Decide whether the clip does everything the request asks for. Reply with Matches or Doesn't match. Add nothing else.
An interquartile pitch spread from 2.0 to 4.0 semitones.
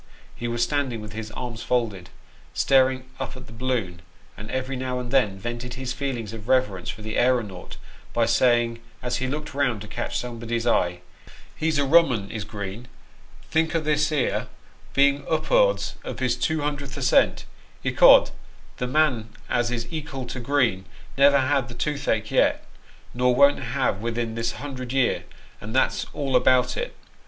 Matches